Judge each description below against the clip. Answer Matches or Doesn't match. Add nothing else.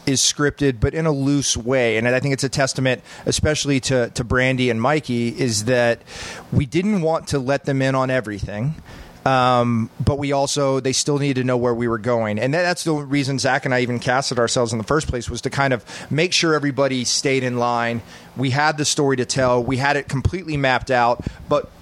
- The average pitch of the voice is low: Matches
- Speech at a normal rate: Doesn't match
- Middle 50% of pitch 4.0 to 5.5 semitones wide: Doesn't match